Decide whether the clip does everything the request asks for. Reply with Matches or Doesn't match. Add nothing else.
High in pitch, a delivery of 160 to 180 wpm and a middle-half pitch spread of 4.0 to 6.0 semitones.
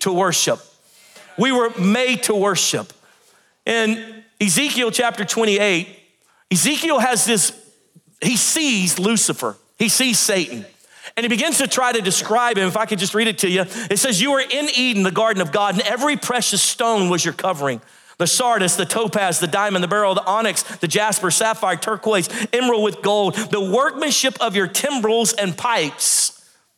Doesn't match